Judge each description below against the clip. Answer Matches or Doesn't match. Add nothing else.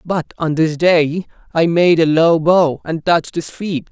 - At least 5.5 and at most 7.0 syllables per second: Doesn't match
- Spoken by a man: Matches